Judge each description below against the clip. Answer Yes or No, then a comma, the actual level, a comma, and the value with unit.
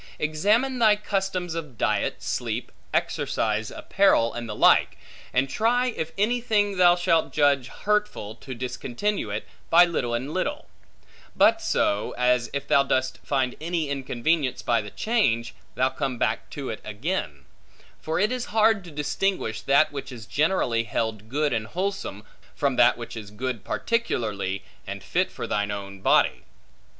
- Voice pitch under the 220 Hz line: Yes, medium, 140 Hz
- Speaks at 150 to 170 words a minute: Yes, average, 160 wpm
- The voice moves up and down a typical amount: No, wide, 8.2 semitones